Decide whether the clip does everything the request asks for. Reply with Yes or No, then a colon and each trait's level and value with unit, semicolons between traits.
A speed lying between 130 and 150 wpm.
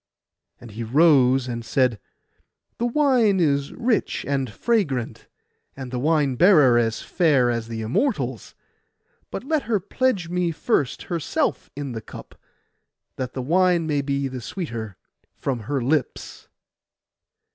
Yes: slow, 135 wpm